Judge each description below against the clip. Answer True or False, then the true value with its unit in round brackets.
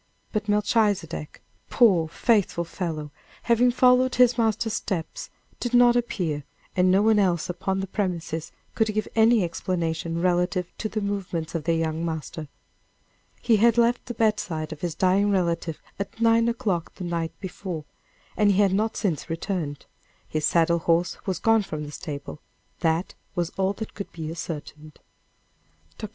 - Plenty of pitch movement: False (4.7 semitones)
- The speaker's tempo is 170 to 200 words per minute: False (160 wpm)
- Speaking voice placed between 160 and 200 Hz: True (185 Hz)